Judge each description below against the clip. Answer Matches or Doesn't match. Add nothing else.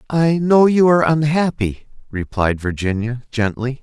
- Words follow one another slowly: Matches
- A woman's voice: Doesn't match